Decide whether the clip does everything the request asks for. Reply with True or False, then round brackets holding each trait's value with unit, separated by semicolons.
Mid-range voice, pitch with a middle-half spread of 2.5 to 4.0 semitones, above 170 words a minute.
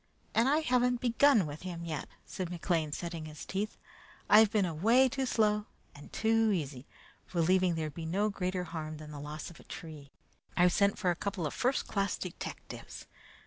False (180 Hz; 5.2 semitones; 185 wpm)